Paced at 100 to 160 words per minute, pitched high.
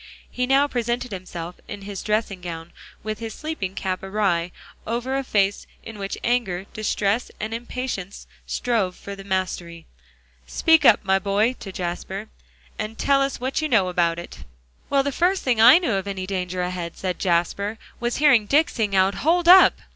No: average, 175 wpm; high, 205 Hz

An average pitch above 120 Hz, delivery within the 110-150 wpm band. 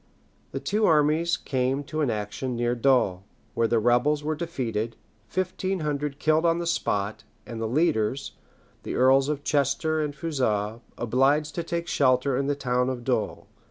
No: low, 135 Hz; average, 165 wpm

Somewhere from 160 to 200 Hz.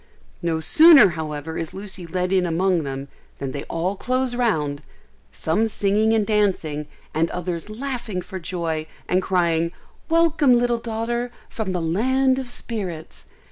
Yes: high, 190 Hz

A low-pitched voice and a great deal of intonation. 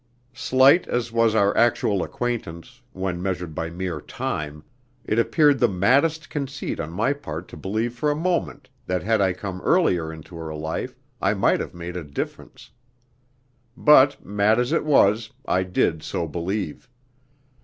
Yes: low, 100 Hz; wide, 6.3 semitones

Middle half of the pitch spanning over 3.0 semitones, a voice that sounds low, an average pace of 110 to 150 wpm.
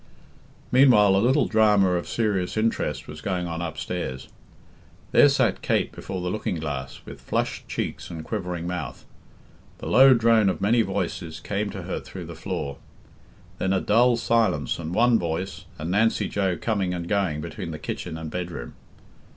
No: average, 4.8 semitones; very low, 95 Hz; average, 165 wpm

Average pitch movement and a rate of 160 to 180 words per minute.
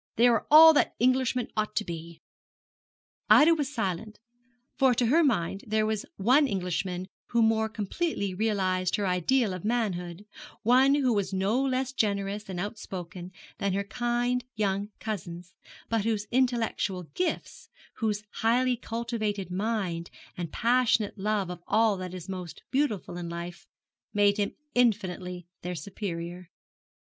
No: average, 4.5 semitones; average, 140 wpm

